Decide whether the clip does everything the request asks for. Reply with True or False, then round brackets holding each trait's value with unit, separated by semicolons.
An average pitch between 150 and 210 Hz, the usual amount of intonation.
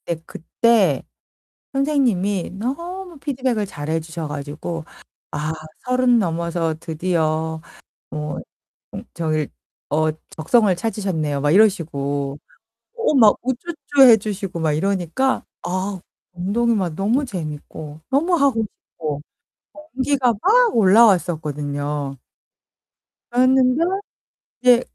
False (190 Hz; 8.0 semitones)